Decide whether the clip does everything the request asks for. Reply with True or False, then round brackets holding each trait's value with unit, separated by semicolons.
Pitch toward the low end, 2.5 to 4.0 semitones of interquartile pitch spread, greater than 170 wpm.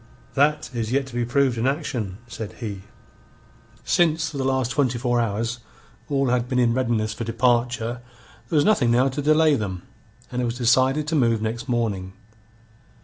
True (125 Hz; 3.0 semitones; 180 wpm)